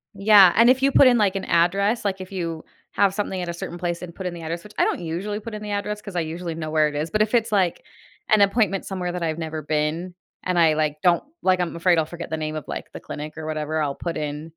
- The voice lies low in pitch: No, medium, 175 Hz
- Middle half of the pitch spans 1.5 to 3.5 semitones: No, average, 4.0 semitones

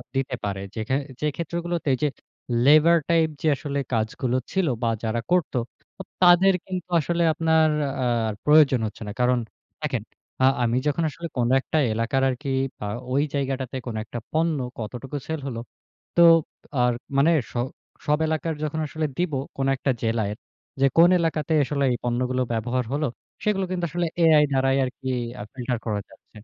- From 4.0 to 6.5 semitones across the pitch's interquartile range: Yes, average, 4.7 semitones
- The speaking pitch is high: No, medium, 140 Hz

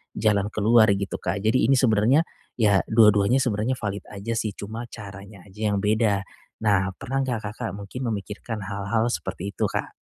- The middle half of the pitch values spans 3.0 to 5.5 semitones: No, narrow, 2.4 semitones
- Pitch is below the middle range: Yes, low, 105 Hz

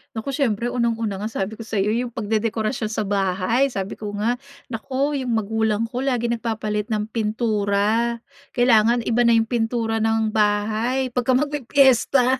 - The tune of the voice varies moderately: No, narrow, 2.3 semitones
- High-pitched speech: Yes, high, 225 Hz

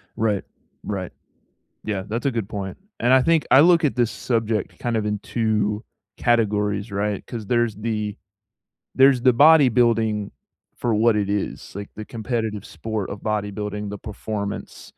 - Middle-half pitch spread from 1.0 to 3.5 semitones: Yes, narrow, 2.4 semitones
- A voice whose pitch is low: Yes, low, 110 Hz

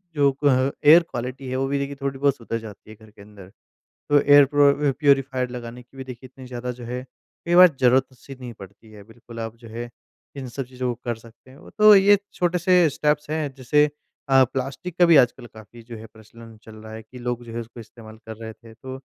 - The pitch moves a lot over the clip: No, average, 3.4 semitones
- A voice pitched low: Yes, low, 125 Hz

